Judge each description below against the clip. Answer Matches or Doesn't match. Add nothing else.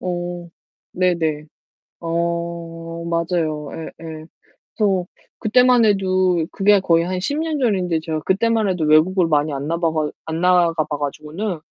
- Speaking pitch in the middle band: Matches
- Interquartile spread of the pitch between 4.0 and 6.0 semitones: Doesn't match